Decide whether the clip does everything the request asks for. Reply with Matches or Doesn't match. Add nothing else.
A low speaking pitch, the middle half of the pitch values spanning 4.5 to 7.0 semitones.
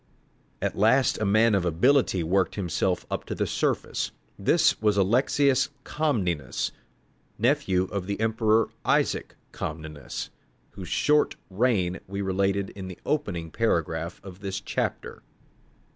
Doesn't match